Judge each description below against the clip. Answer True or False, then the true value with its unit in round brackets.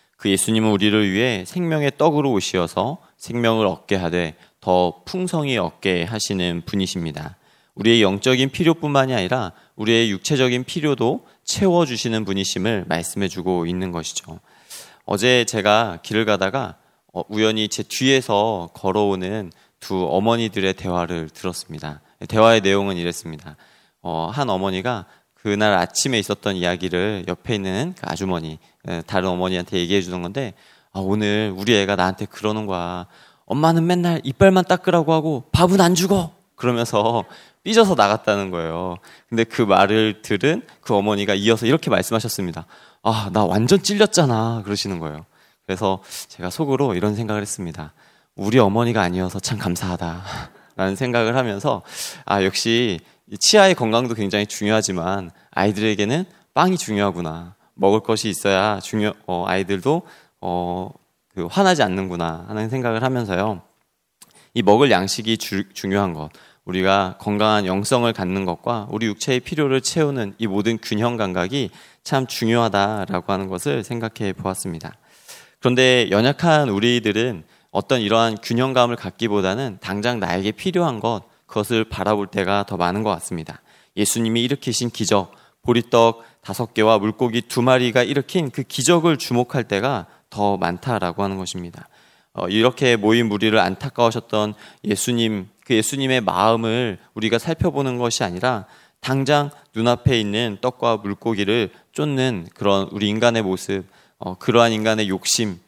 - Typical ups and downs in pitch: True (4.4 semitones)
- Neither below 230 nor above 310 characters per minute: False (335 characters per minute)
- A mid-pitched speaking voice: False (105 Hz)